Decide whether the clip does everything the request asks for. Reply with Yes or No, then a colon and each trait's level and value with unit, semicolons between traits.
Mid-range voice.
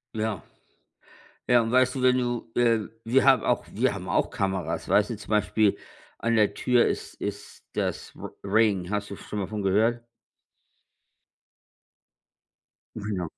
No: low, 110 Hz